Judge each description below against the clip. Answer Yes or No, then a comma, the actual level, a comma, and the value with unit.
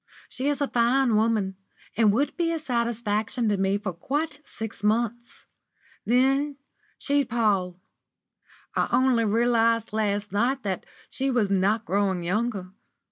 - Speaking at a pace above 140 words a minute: No, slow, 135 wpm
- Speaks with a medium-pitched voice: No, high, 230 Hz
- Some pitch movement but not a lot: Yes, average, 4.0 semitones